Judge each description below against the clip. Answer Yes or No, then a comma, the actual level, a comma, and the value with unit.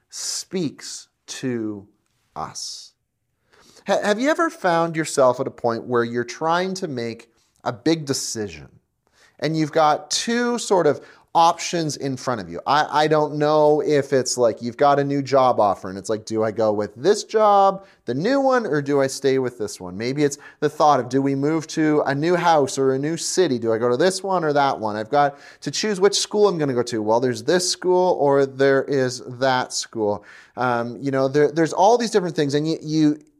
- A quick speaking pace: Yes, fast, 215 wpm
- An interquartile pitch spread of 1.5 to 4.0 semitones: No, average, 5.0 semitones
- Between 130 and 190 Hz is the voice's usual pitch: Yes, medium, 140 Hz